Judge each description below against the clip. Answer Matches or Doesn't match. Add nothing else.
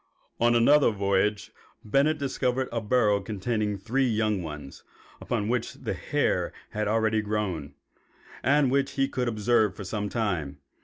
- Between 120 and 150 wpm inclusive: Matches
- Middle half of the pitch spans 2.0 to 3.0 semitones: Doesn't match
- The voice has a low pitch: Matches